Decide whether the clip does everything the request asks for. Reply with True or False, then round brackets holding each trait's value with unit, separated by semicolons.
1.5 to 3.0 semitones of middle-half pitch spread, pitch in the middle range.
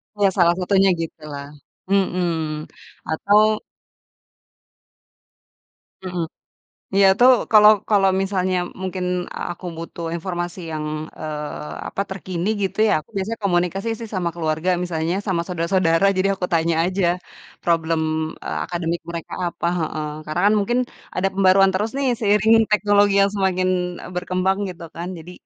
True (2.7 semitones; 180 Hz)